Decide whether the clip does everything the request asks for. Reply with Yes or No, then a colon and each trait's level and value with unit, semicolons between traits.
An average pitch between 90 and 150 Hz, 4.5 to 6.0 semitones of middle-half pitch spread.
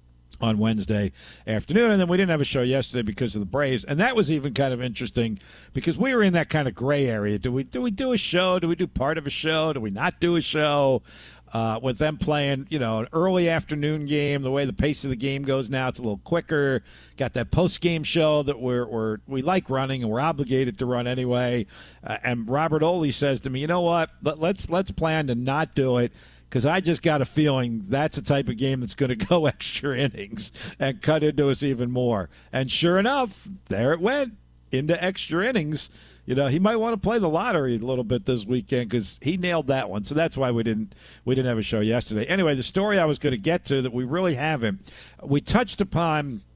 Yes: medium, 140 Hz; average, 4.9 semitones